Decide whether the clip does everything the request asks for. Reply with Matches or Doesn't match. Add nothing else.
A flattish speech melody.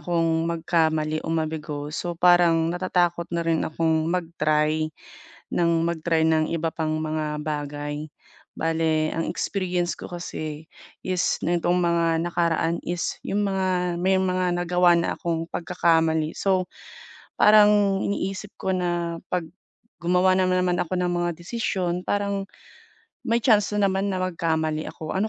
Matches